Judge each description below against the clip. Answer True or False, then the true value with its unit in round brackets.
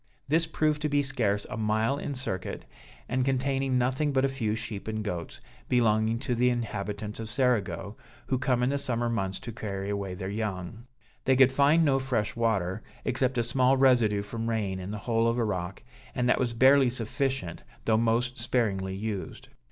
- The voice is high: False (115 Hz)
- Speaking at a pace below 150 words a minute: False (190 wpm)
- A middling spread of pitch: True (4.0 semitones)